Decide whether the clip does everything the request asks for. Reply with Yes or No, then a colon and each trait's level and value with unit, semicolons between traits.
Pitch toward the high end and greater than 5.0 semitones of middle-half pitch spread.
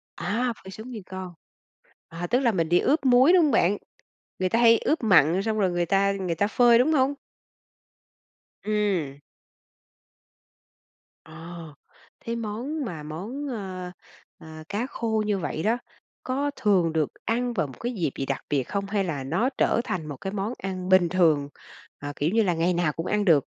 Yes: high, 195 Hz; wide, 5.4 semitones